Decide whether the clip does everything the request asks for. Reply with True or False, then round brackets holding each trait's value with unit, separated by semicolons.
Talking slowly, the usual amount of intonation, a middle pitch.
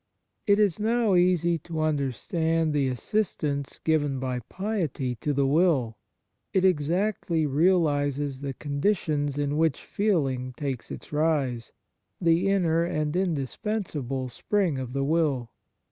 True (125 wpm; 4.4 semitones; 155 Hz)